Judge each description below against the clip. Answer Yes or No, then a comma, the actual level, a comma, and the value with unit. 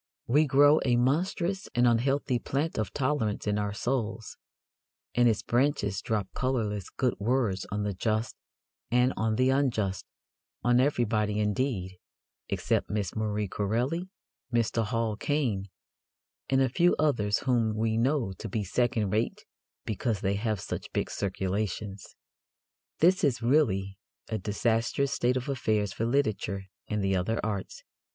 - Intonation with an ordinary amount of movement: Yes, average, 4.0 semitones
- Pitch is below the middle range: Yes, low, 115 Hz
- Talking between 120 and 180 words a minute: Yes, average, 145 wpm